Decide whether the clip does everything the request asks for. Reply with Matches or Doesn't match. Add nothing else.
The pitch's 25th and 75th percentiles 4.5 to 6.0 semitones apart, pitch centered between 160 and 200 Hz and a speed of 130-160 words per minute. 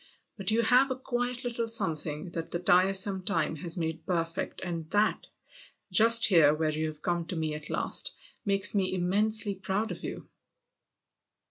Matches